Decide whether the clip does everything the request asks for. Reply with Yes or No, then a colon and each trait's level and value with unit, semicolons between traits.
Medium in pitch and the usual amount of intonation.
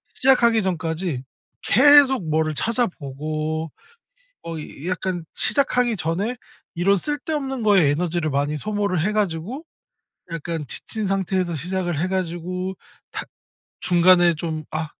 Yes: medium, 180 Hz; average, 4.7 semitones